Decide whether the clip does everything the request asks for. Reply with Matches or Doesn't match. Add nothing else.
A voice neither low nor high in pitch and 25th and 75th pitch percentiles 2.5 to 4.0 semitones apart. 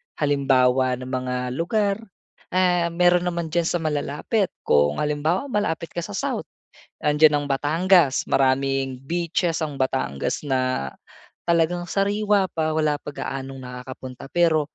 Doesn't match